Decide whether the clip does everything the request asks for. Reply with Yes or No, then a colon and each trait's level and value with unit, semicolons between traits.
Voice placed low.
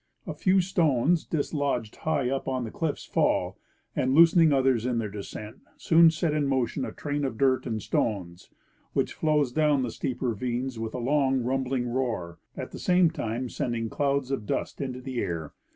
Yes: low, 130 Hz